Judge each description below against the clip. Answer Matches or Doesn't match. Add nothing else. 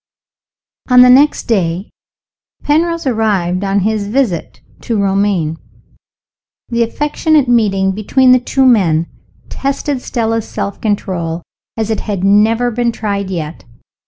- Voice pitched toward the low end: Doesn't match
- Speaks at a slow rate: Matches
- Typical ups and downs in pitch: Matches